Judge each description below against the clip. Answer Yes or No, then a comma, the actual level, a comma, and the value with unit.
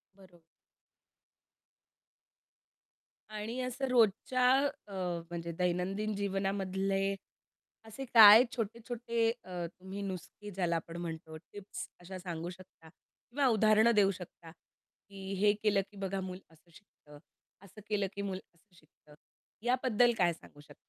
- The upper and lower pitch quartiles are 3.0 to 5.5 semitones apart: Yes, average, 3.3 semitones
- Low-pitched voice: No, high, 195 Hz